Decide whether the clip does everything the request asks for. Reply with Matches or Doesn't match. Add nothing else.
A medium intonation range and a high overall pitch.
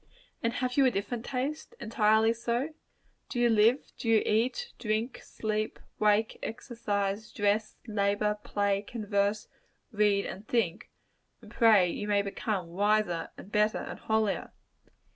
Doesn't match